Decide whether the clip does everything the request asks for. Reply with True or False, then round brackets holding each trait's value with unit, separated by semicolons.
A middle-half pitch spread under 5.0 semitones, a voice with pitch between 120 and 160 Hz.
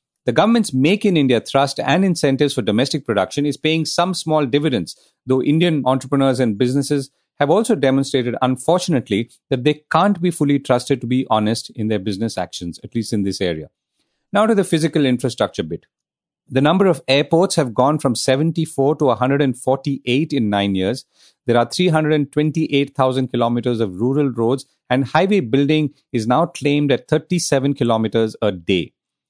True (3.9 semitones; 135 Hz)